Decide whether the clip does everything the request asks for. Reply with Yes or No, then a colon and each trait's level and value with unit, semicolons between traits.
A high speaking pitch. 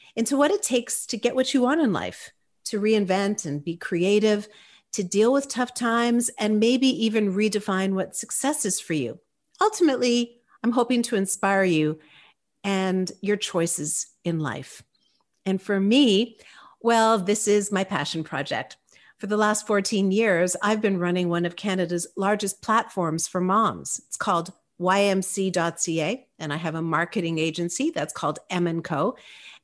Yes: high, 205 Hz